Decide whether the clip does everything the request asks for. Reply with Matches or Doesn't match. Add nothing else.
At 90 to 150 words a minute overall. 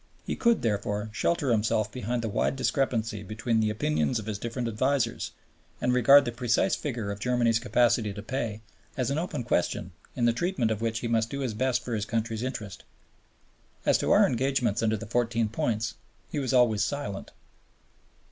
Doesn't match